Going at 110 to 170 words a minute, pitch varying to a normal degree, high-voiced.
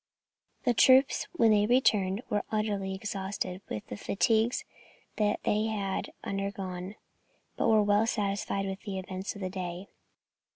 No: average, 140 wpm; narrow, 2.1 semitones; high, 200 Hz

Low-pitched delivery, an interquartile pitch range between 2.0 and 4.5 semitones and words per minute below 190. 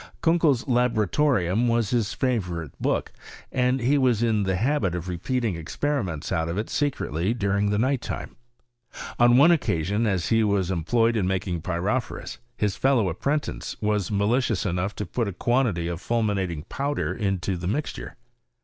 No: low, 105 Hz; average, 5.3 semitones; average, 160 wpm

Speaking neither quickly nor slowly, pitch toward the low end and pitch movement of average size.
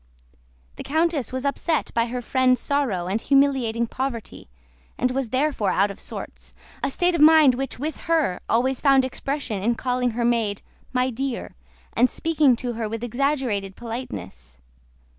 No: average, 160 wpm; very high, 255 Hz; average, 3.4 semitones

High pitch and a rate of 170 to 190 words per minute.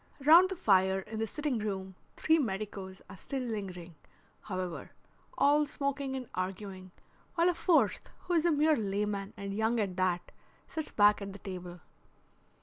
No: high, 210 Hz; average, 160 wpm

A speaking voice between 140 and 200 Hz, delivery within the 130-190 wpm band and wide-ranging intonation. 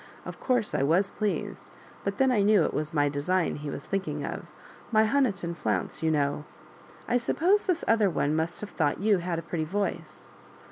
No: medium, 185 Hz; fast, 205 wpm; wide, 5.7 semitones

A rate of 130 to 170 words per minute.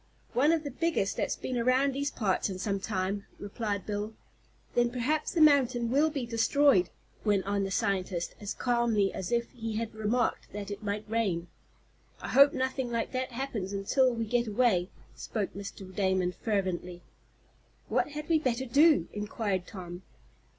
Yes: average, 165 wpm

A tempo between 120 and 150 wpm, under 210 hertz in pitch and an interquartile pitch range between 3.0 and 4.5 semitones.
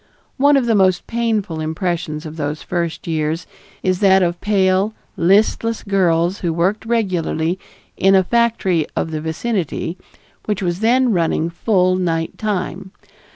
Yes: average, 145 wpm; medium, 185 Hz; average, 4.1 semitones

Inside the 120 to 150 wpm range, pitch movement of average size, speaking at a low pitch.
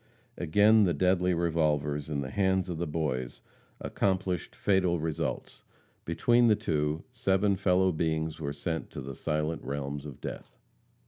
Yes: average, 145 wpm; average, 4.1 semitones; very low, 80 Hz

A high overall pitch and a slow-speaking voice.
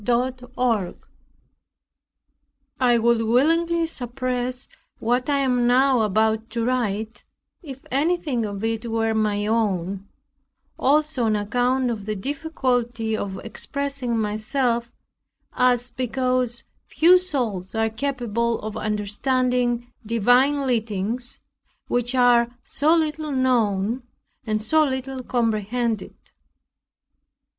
Yes: high, 245 Hz; slow, 105 wpm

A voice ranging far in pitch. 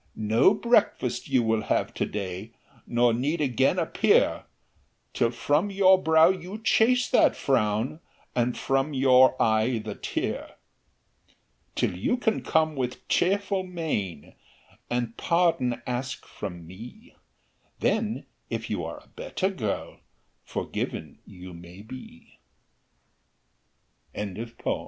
Yes: wide, 8.3 semitones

